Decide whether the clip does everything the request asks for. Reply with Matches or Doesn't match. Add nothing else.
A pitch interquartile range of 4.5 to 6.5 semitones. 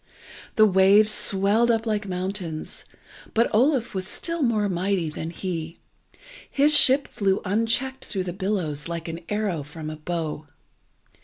Matches